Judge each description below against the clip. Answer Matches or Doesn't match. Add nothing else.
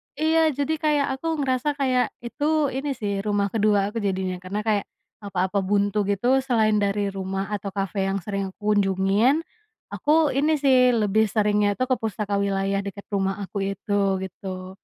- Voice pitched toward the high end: Matches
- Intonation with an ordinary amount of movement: Matches